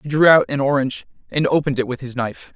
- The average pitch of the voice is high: No, low, 135 Hz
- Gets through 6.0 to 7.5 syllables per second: Yes, 7.0 syllables/s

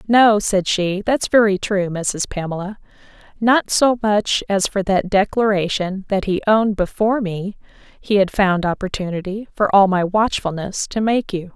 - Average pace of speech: Yes, average, 160 wpm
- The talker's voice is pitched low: No, high, 200 Hz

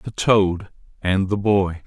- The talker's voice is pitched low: Yes, very low, 95 Hz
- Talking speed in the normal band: Yes, average, 160 wpm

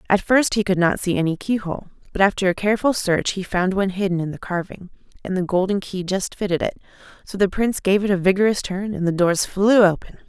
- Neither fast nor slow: No, fast, 235 wpm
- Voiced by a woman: Yes, female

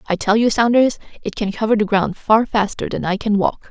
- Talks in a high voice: Yes, high, 210 Hz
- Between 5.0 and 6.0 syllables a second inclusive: Yes, 5.4 syllables/s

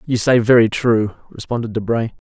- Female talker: No, male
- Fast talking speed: No, average, 155 wpm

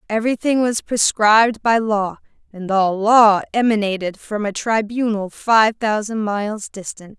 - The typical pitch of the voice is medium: No, high, 215 Hz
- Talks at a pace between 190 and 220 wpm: No, average, 140 wpm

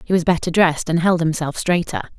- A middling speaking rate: No, fast, 220 wpm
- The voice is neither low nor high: Yes, medium, 170 Hz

